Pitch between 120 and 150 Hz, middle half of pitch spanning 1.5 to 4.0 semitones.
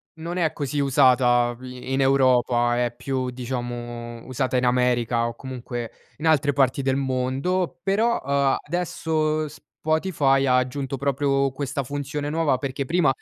Yes: low, 135 Hz; average, 2.7 semitones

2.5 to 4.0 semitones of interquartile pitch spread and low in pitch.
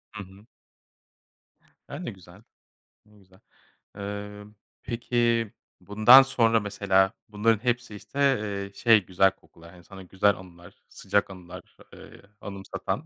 Yes: average, 2.9 semitones; low, 105 Hz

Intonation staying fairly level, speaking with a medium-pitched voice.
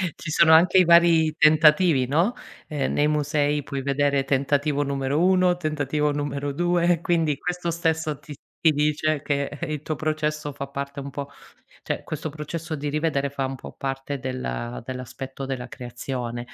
Yes: narrow, 2.3 semitones; medium, 145 Hz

